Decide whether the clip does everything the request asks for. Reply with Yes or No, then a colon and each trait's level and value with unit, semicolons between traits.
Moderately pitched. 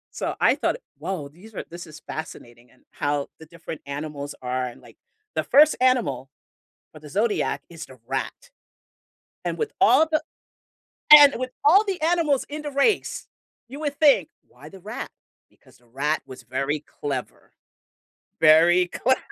Yes: medium, 165 Hz